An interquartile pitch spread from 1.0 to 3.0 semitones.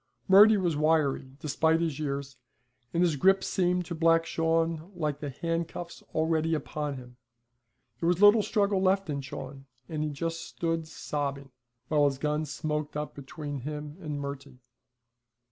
Yes: average, 2.7 semitones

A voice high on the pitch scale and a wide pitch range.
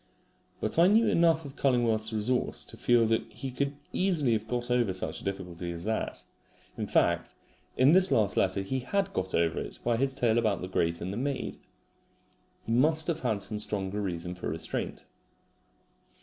No: low, 115 Hz; wide, 6.0 semitones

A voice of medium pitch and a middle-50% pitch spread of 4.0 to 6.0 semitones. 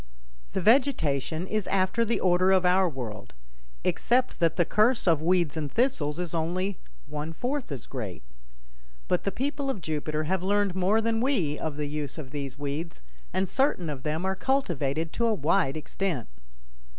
Yes: medium, 175 Hz; wide, 5.4 semitones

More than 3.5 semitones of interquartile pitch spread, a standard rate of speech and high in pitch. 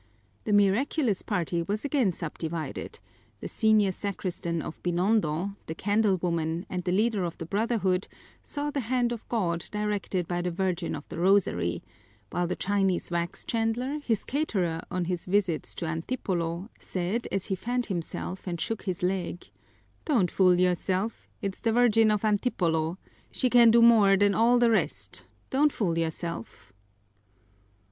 Yes: average, 4.4 semitones; average, 155 wpm; high, 195 Hz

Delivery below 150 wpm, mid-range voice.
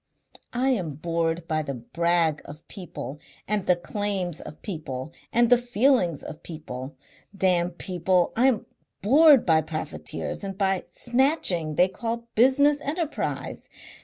Yes: average, 140 wpm; medium, 180 Hz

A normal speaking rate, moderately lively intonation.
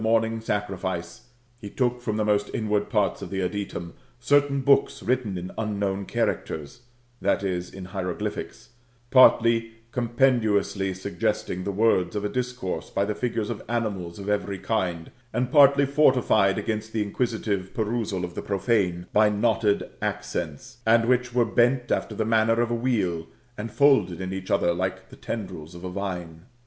Yes: average, 160 wpm; average, 3.8 semitones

